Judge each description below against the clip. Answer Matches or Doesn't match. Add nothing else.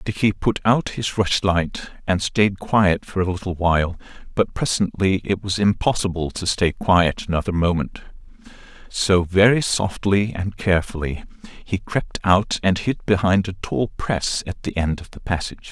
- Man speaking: Matches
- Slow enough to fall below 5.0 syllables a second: Matches